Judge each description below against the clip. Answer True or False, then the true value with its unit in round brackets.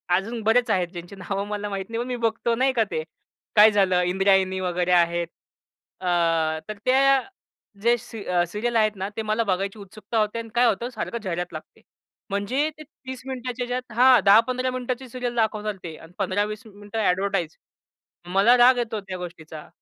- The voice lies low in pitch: False (215 Hz)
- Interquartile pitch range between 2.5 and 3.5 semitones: False (4.0 semitones)